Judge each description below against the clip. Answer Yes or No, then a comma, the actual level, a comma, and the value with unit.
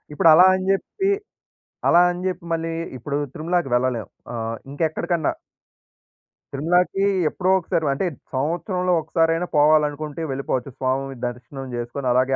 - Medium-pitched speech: Yes, medium, 155 Hz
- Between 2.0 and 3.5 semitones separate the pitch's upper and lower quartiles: No, average, 4.6 semitones